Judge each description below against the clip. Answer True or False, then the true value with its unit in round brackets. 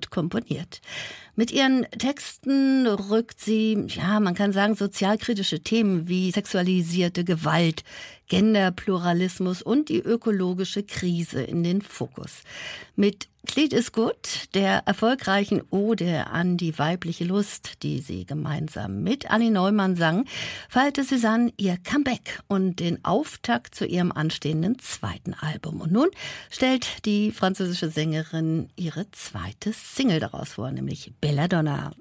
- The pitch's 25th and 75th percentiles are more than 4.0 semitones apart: True (4.4 semitones)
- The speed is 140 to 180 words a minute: False (125 wpm)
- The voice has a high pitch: True (195 Hz)